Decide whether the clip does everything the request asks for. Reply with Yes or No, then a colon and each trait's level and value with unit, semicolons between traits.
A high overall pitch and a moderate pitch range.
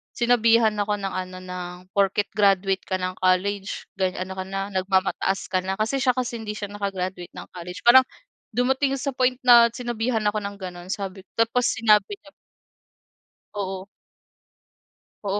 Yes: high, 200 Hz; average, 3.6 semitones